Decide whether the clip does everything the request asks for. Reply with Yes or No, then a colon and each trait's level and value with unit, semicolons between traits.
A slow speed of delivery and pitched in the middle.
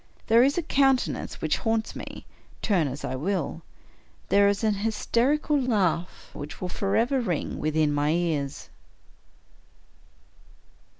No: slow, 125 wpm; high, 200 Hz